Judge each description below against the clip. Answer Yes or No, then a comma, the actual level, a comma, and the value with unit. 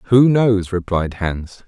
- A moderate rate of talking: Yes, average, 145 wpm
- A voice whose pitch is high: No, low, 100 Hz